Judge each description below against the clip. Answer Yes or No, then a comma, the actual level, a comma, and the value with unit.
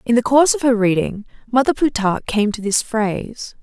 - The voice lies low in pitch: No, high, 230 Hz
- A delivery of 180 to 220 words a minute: Yes, average, 200 wpm